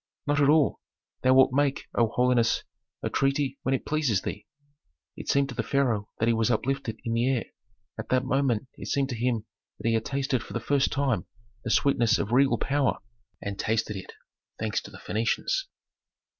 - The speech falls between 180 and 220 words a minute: Yes, average, 195 wpm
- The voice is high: No, low, 125 Hz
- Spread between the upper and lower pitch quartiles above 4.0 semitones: No, average, 3.4 semitones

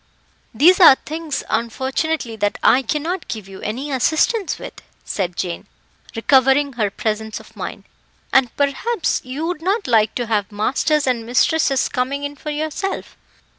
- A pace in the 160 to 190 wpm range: No, average, 150 wpm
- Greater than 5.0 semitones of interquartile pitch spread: Yes, wide, 5.5 semitones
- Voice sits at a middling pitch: No, very high, 265 Hz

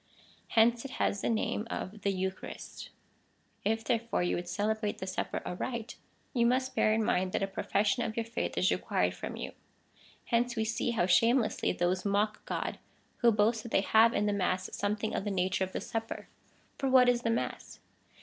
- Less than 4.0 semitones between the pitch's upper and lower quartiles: Yes, average, 3.1 semitones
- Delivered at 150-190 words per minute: No, average, 200 wpm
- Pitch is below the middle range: No, high, 220 Hz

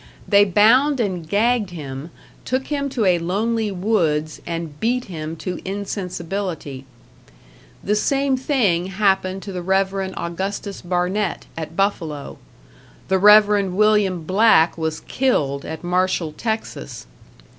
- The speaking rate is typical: No, slow, 125 wpm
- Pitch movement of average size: Yes, average, 4.0 semitones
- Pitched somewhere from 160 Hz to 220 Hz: Yes, high, 190 Hz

